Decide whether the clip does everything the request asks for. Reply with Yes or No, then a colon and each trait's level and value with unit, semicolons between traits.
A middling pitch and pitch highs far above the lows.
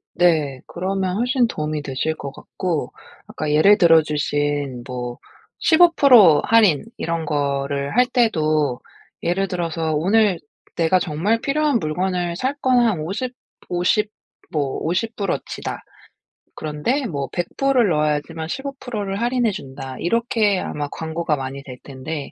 Yes: medium, 170 Hz; wide, 6.6 semitones